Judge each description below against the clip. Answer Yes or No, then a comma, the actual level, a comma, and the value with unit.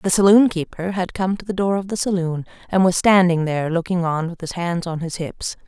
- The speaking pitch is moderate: Yes, medium, 180 Hz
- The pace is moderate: No, fast, 245 wpm